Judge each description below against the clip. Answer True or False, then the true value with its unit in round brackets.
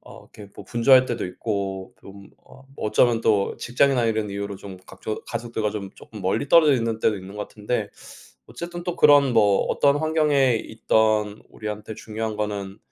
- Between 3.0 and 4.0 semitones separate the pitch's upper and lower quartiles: True (3.7 semitones)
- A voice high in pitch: False (110 Hz)